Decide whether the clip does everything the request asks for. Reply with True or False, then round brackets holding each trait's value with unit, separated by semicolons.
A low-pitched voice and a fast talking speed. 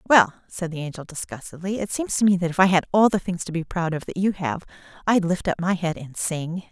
False (175 Hz; 270 wpm)